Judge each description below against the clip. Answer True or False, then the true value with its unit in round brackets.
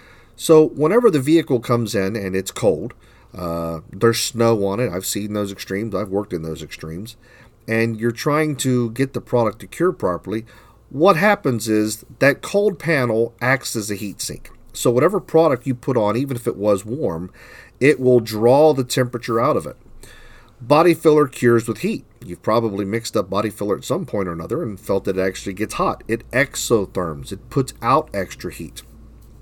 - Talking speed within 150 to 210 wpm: True (190 wpm)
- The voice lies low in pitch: True (115 Hz)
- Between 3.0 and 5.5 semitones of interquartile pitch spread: True (4.1 semitones)